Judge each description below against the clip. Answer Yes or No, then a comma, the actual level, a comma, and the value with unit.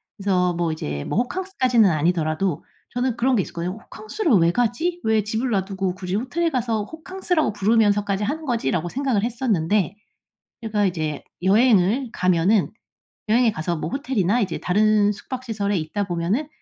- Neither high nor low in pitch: No, high, 210 Hz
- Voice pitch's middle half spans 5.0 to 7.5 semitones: Yes, average, 5.3 semitones